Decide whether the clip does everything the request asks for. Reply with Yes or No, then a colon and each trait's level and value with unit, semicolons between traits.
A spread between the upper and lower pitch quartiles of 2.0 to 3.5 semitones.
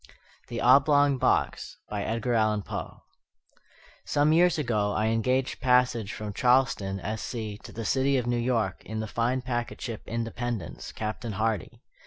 Yes: average, 2.9 semitones